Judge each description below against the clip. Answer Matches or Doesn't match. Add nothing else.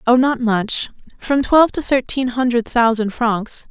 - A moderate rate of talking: Matches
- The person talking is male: Doesn't match